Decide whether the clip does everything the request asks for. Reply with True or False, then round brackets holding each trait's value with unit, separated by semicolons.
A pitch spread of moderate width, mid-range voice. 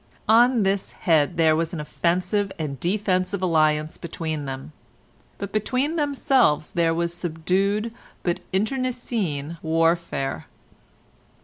True (4.5 semitones; 175 Hz)